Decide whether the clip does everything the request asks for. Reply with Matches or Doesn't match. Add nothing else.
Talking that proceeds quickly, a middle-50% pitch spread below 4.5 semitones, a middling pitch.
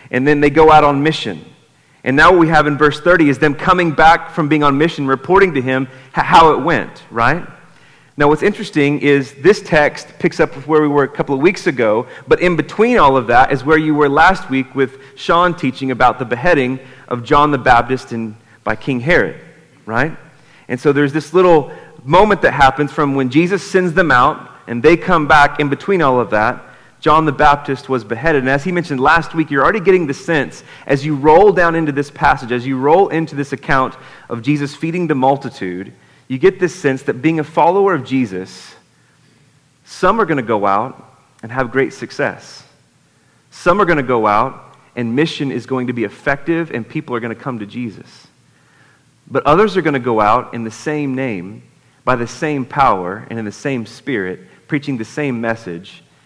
Matches